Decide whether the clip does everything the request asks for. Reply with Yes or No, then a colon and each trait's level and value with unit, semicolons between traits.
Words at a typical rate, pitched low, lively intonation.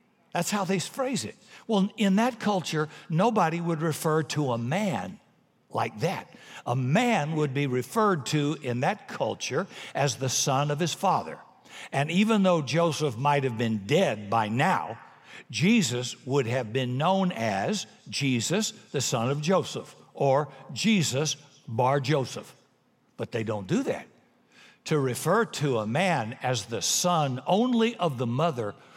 No: average, 155 wpm; medium, 155 Hz; wide, 6.2 semitones